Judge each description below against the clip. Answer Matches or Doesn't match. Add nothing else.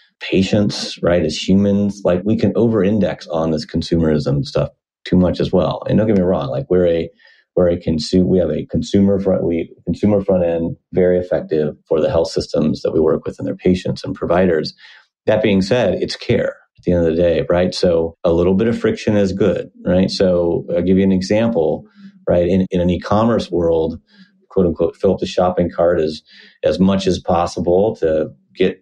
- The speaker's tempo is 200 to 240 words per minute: Matches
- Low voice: Matches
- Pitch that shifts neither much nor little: Matches